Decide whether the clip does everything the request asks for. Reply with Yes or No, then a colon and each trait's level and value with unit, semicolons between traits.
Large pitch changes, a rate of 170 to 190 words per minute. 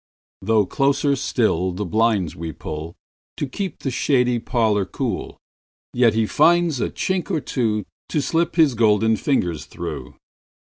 No: wide, 6.4 semitones; slow, 135 wpm